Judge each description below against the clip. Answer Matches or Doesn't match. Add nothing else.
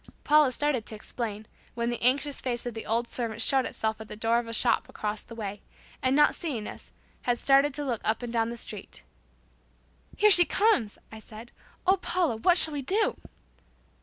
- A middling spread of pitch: Matches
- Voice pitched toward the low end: Doesn't match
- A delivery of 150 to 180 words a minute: Doesn't match